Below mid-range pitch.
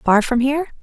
No: very high, 260 Hz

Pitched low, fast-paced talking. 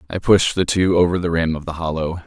Yes: very low, 85 Hz; fast, 265 wpm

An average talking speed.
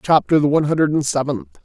No: fast, 220 wpm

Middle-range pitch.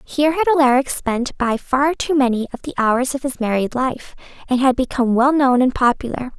No: very high, 260 Hz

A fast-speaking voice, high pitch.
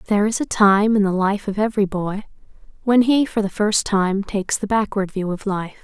Yes: fast, 225 wpm; high, 205 Hz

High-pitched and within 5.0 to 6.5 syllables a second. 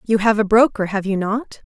Yes: high, 210 Hz; 5.3 syllables/s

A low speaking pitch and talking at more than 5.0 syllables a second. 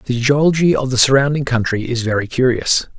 Yes: low, 130 Hz; 5.5 syllables/s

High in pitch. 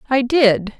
Yes: high, 240 Hz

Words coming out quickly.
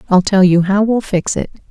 Yes: fast, 245 wpm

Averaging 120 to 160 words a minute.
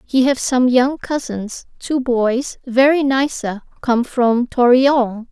Yes: average, 145 wpm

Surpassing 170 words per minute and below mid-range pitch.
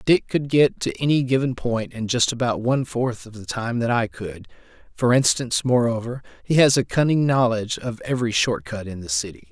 Yes: average, 200 wpm; low, 120 Hz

